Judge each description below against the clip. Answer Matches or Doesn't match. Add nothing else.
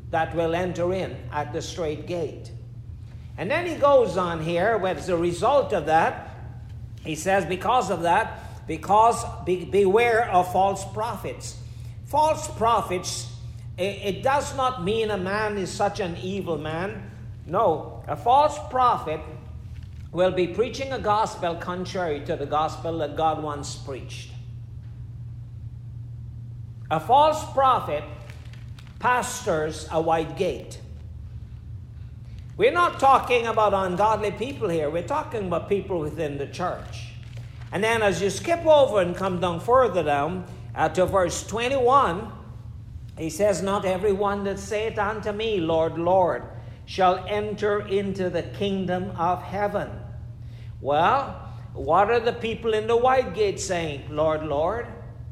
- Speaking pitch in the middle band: Matches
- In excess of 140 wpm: Doesn't match